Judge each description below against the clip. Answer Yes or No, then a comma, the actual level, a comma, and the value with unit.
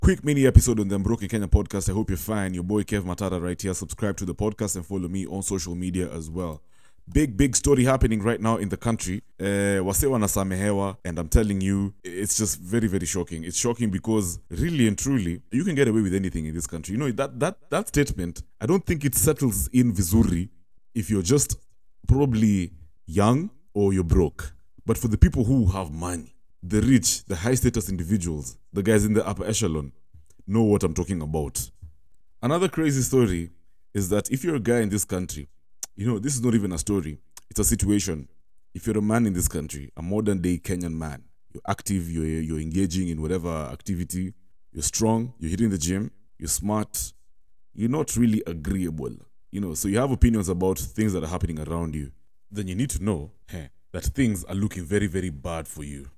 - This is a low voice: Yes, low, 100 Hz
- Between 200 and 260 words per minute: Yes, fast, 205 wpm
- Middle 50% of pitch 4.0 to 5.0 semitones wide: Yes, average, 4.4 semitones